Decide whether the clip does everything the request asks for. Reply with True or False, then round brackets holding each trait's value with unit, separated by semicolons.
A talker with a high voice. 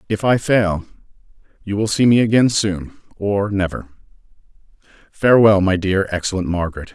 False (100 Hz)